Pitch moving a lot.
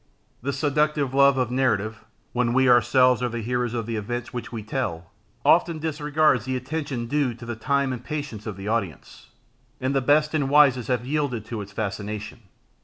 No: average, 3.6 semitones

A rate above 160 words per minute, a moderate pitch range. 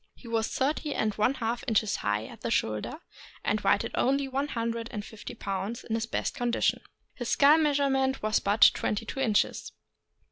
Yes: average, 180 wpm; average, 3.9 semitones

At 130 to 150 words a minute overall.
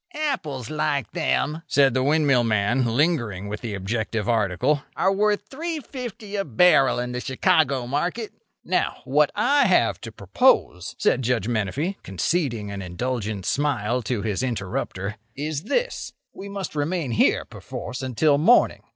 Yes: average, 145 wpm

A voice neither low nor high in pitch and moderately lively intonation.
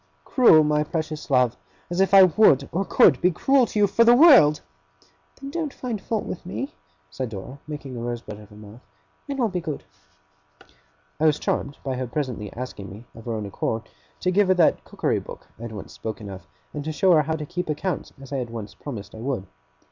No: medium, 145 Hz; wide, 7.9 semitones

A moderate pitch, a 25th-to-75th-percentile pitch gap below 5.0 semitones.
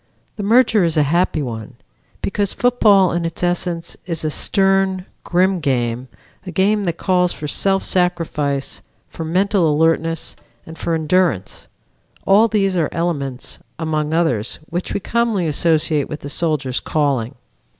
Yes: medium, 170 Hz; average, 4.0 semitones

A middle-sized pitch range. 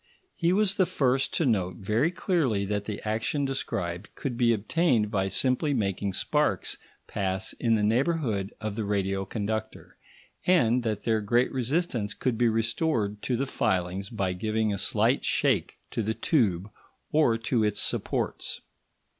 Yes: average, 4.5 semitones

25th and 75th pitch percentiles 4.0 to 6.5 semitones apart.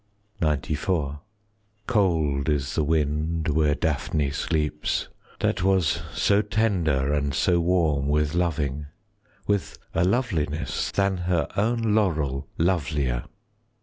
Yes: average, 4.4 semitones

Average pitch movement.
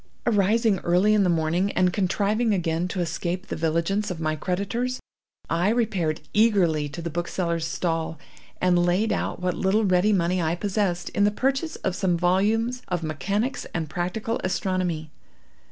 Yes: average, 3.5 semitones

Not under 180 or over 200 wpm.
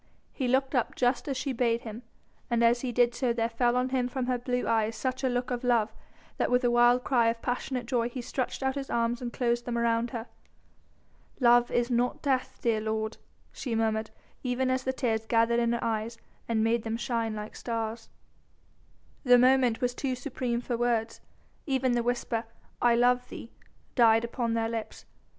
Yes: average, 195 wpm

